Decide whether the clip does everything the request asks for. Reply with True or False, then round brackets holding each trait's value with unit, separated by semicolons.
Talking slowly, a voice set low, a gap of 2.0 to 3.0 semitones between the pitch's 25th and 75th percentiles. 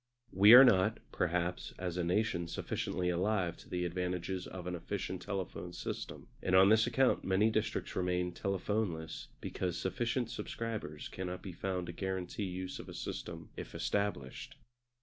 False (155 wpm; 95 Hz; 2.6 semitones)